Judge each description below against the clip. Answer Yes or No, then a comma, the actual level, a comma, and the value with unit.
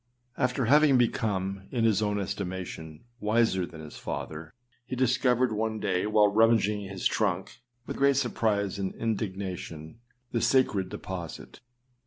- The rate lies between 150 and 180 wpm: No, slow, 135 wpm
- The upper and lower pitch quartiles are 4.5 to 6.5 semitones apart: No, average, 3.8 semitones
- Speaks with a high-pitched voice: No, low, 105 Hz